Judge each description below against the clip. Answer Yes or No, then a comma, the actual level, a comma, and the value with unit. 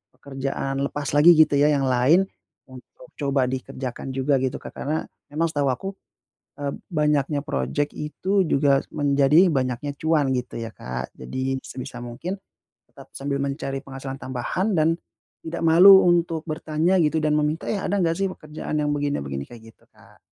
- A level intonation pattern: No, average, 3.2 semitones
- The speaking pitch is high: No, medium, 145 Hz